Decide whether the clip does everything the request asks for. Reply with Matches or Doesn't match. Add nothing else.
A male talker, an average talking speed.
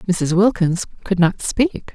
Doesn't match